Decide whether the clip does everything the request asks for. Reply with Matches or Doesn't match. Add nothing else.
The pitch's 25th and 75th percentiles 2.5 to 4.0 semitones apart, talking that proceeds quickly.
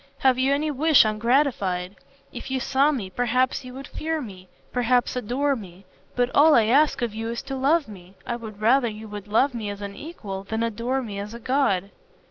Doesn't match